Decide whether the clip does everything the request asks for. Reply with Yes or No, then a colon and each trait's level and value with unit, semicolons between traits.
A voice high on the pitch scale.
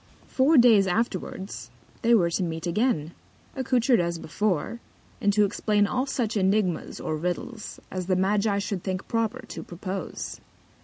Yes: high, 200 Hz